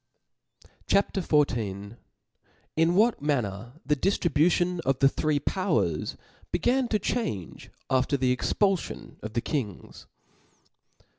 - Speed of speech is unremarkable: No, slow, 105 wpm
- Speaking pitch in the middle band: Yes, medium, 145 Hz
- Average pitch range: No, wide, 7.1 semitones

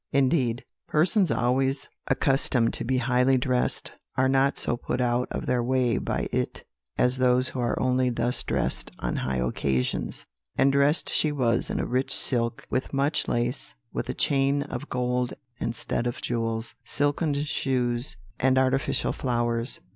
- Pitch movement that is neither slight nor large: No, narrow, 2.1 semitones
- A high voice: No, low, 125 Hz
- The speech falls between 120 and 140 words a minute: No, average, 160 wpm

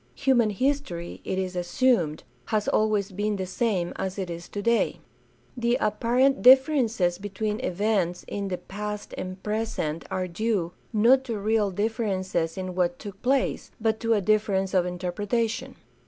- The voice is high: Yes, high, 205 Hz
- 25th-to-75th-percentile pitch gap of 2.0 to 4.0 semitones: Yes, average, 3.7 semitones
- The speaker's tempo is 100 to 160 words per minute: Yes, average, 150 wpm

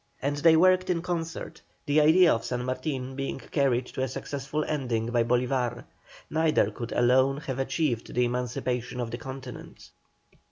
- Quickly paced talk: No, average, 160 wpm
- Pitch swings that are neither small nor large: Yes, average, 3.7 semitones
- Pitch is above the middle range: No, low, 130 Hz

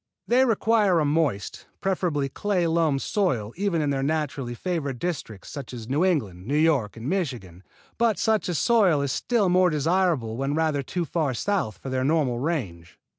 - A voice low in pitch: No, medium, 150 Hz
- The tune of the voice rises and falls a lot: Yes, wide, 5.7 semitones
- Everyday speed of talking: Yes, average, 175 wpm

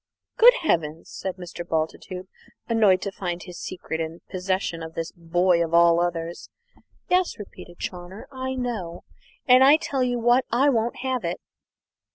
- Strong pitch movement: Yes, wide, 6.3 semitones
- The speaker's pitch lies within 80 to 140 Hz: No, medium, 185 Hz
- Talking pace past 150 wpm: Yes, average, 160 wpm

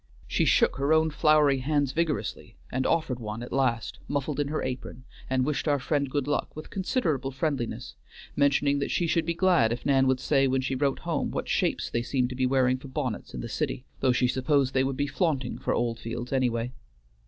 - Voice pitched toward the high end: No, low, 135 Hz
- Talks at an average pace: No, fast, 210 wpm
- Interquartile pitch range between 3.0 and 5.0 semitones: No, narrow, 2.6 semitones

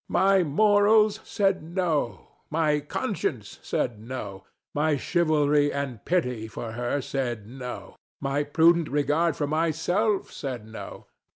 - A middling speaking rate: No, slow, 120 wpm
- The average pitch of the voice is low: No, medium, 150 Hz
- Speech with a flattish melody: No, average, 5.3 semitones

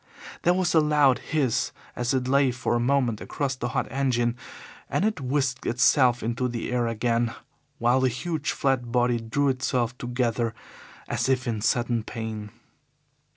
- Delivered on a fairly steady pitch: Yes, narrow, 2.3 semitones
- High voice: No, low, 125 Hz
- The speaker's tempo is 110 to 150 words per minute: No, average, 160 wpm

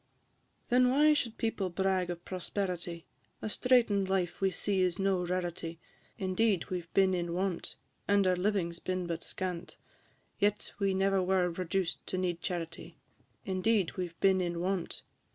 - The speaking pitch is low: No, medium, 185 Hz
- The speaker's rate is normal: Yes, average, 170 wpm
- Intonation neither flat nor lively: No, narrow, 2.0 semitones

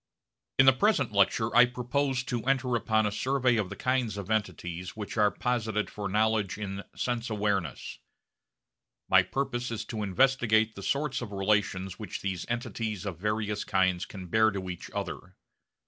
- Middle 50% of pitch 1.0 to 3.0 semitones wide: No, average, 3.7 semitones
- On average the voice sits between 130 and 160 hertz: No, low, 110 Hz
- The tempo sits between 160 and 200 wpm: Yes, average, 165 wpm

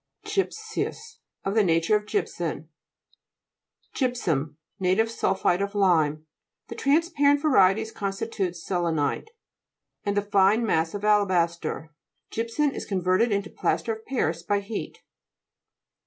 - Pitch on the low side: No, high, 200 Hz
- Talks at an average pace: No, slow, 125 wpm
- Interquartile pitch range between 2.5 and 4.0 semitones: No, average, 4.4 semitones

